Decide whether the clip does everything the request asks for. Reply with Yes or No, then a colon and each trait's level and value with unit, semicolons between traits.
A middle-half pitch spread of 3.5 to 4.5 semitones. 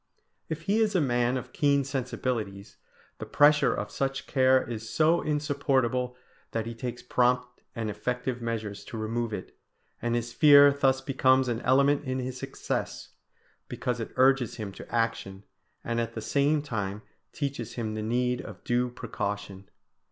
No: average, 3.0 semitones